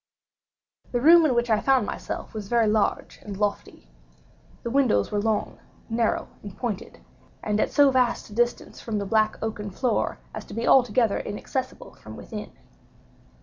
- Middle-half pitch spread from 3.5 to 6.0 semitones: No, average, 3.0 semitones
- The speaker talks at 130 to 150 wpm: No, average, 165 wpm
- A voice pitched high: Yes, high, 225 Hz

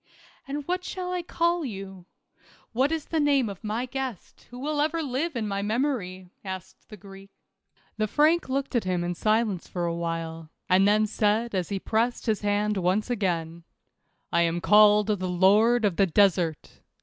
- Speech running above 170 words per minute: Yes, average, 180 wpm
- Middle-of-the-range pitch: No, high, 210 Hz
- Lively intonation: Yes, wide, 5.7 semitones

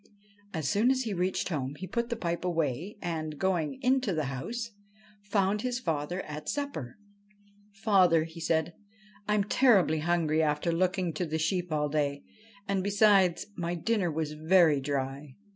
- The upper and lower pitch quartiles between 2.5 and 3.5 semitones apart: No, average, 4.7 semitones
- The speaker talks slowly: No, average, 170 wpm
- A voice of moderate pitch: Yes, medium, 175 Hz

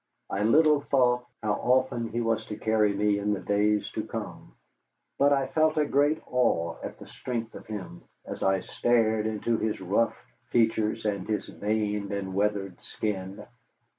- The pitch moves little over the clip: No, average, 3.1 semitones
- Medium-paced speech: Yes, average, 165 wpm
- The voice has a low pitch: Yes, low, 110 Hz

